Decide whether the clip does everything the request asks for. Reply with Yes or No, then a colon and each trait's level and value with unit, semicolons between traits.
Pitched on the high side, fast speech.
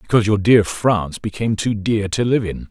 No: low, 105 Hz; fast, 220 wpm